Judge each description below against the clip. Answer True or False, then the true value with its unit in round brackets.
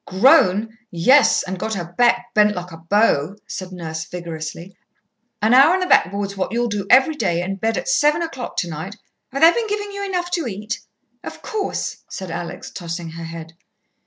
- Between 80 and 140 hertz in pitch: False (200 Hz)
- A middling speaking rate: True (190 wpm)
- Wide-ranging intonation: True (7.3 semitones)